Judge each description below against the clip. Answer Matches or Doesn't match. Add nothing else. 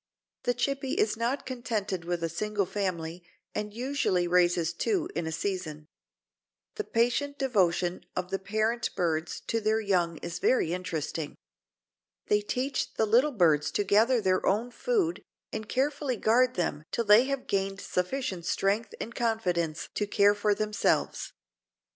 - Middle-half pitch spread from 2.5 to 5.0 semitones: Doesn't match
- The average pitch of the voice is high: Matches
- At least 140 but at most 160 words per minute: Matches